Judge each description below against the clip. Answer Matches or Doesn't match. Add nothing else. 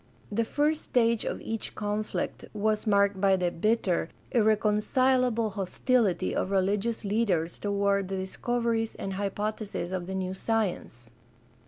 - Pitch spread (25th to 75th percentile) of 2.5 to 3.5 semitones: Matches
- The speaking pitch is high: Matches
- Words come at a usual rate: Doesn't match